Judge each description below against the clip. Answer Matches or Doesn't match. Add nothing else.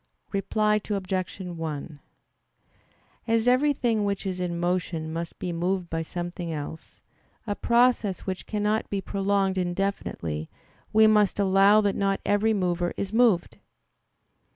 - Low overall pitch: Doesn't match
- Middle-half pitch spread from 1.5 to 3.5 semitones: Matches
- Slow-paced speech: Matches